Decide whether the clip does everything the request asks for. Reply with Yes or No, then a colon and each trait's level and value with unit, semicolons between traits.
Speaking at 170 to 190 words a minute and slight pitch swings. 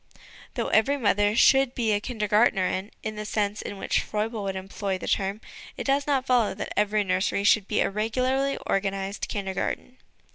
No: average, 180 wpm; average, 3.3 semitones